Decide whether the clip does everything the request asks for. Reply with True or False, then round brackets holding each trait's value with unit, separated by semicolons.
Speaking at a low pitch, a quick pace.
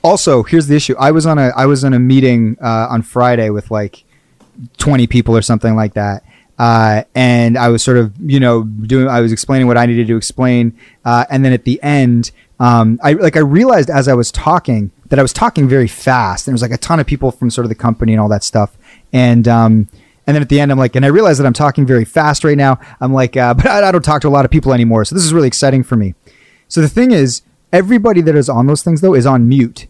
True (125 Hz; 265 wpm)